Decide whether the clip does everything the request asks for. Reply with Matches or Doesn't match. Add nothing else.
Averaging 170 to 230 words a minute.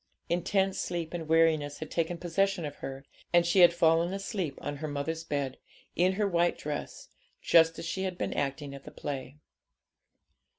Matches